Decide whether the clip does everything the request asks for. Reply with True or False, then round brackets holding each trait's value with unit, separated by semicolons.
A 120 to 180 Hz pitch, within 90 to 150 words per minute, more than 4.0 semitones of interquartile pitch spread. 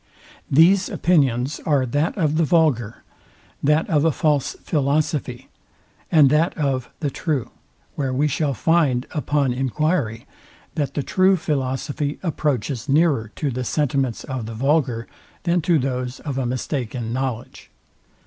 False (140 Hz; 140 wpm; 3.3 semitones)